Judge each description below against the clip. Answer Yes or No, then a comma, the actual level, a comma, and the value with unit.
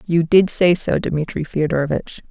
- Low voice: No, medium, 165 Hz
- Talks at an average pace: Yes, average, 155 wpm